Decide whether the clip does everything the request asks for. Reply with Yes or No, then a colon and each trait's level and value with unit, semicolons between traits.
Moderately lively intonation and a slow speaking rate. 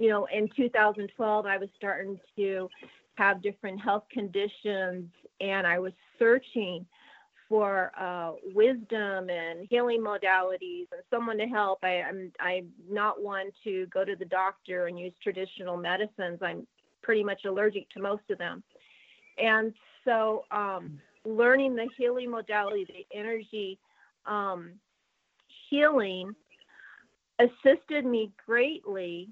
Yes: average, 3.3 semitones; slow, 125 wpm